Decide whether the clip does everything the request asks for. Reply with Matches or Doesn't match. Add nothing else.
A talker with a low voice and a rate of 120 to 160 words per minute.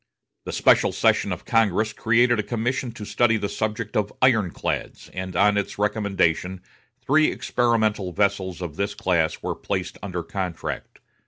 Matches